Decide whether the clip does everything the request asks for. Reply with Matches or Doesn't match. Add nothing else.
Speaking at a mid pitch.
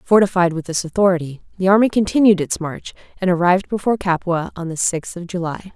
Matches